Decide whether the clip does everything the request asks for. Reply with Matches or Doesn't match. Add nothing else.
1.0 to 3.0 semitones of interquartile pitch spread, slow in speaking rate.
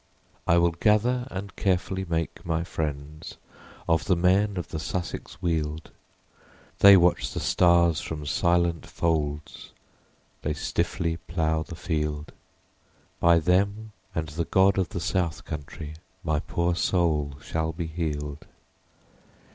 Matches